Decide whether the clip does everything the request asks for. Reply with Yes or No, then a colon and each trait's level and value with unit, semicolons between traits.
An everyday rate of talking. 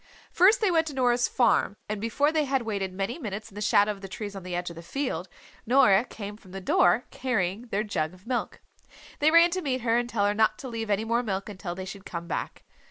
No: fast, 250 wpm